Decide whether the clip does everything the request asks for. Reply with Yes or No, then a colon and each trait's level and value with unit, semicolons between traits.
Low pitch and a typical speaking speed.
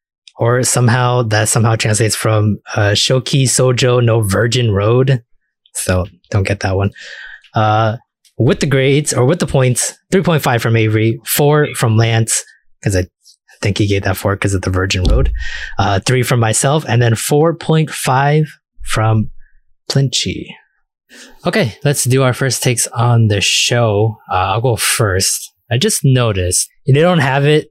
Yes: low, 115 Hz; average, 155 wpm